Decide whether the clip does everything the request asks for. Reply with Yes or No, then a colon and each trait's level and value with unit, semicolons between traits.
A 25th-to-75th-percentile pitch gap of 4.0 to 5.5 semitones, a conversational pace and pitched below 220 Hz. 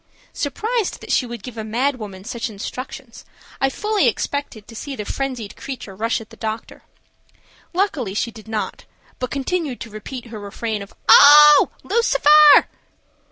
No: average, 4.7 semitones; average, 160 wpm; high, 245 Hz